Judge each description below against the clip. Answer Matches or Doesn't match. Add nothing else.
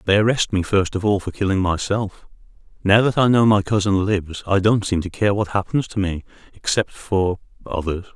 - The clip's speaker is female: Doesn't match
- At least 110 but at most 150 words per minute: Doesn't match